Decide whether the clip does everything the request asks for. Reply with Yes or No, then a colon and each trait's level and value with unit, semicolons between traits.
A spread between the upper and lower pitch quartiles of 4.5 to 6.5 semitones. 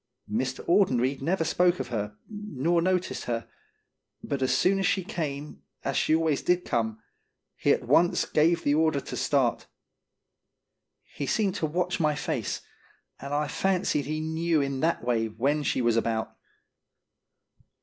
Yes: average, 4.9 semitones